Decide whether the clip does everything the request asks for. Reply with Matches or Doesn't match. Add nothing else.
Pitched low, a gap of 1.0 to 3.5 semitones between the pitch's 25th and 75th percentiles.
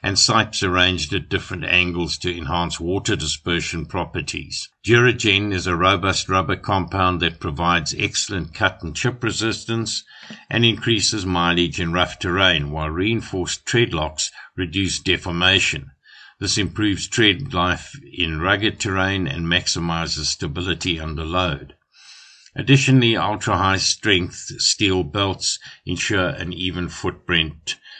Matches